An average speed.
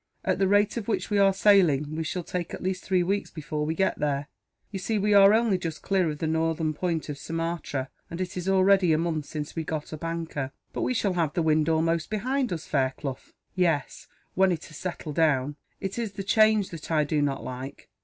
No: fast, 225 wpm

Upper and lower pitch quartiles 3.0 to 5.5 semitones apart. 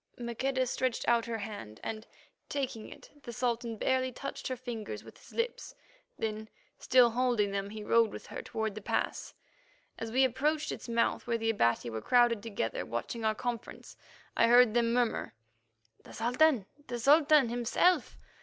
No: narrow, 2.6 semitones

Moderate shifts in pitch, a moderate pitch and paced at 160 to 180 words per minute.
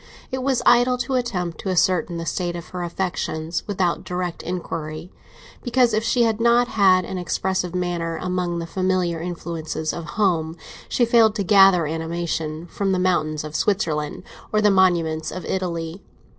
Yes: average, 3.2 semitones; medium, 180 Hz; average, 165 wpm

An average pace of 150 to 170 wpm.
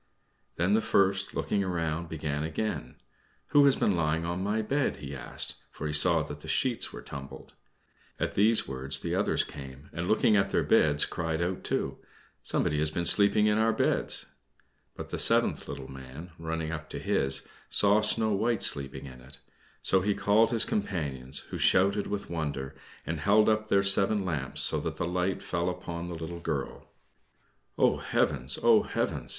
No: average, 180 wpm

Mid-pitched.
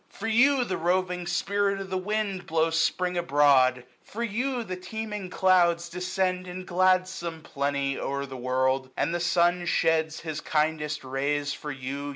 Yes: medium, 175 Hz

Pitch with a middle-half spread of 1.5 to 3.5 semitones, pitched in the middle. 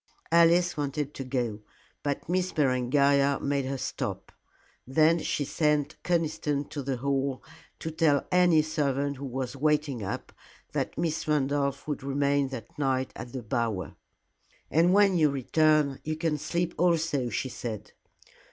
Yes: average, 2.8 semitones; medium, 145 Hz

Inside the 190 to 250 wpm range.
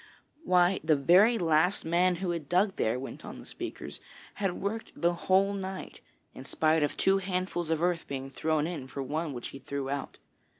Yes: average, 195 wpm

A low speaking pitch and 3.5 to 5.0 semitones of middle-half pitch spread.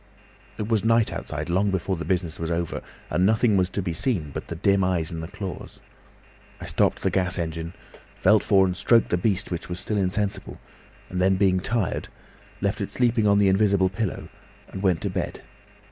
No: very low, 95 Hz; average, 2.7 semitones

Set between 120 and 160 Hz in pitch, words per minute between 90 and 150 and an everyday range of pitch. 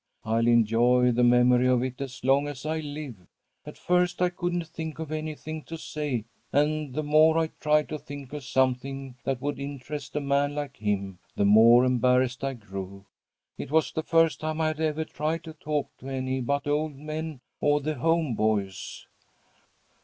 No: medium, 140 Hz; average, 185 wpm; average, 3.7 semitones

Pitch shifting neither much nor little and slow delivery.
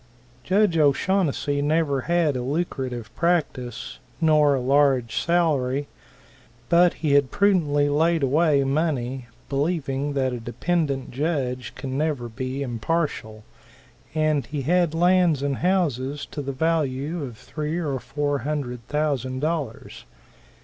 Yes: average, 3.8 semitones; slow, 125 wpm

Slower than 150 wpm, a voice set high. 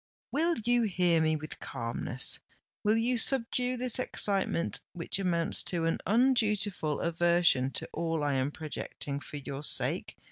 No: average, 140 wpm; medium, 175 Hz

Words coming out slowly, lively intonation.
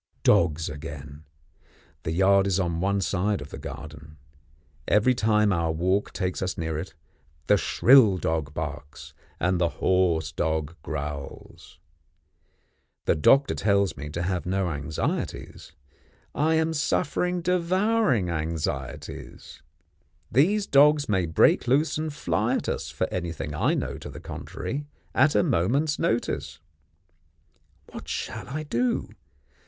Yes: slow, 130 wpm; wide, 8.8 semitones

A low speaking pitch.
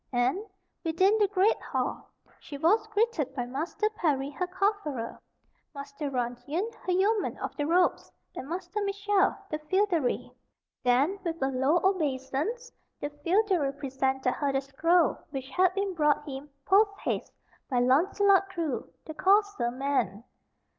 No: very high, 320 Hz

